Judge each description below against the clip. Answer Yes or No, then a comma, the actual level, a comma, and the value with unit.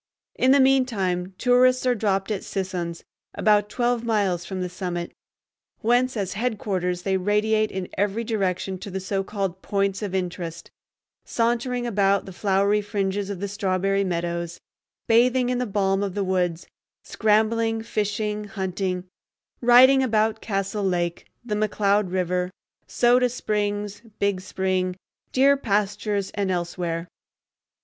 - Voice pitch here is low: No, high, 200 Hz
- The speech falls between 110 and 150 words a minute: Yes, average, 140 wpm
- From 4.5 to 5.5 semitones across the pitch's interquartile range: No, average, 3.0 semitones